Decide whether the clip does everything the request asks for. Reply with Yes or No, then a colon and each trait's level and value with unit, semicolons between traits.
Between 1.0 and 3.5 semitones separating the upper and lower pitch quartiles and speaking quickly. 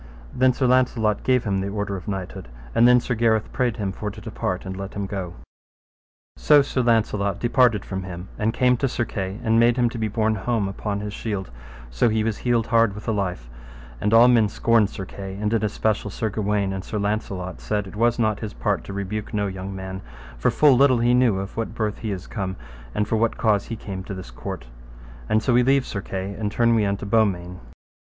Yes: average, 3.0 semitones; fast, 230 wpm